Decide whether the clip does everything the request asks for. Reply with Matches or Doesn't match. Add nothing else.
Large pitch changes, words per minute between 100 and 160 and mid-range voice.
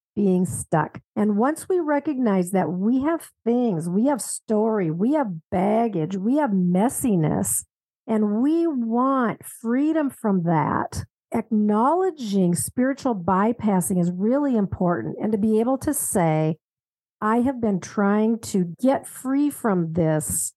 Doesn't match